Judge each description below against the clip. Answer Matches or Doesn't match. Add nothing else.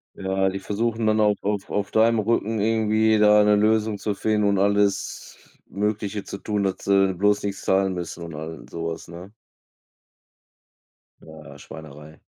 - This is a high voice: Doesn't match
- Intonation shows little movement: Matches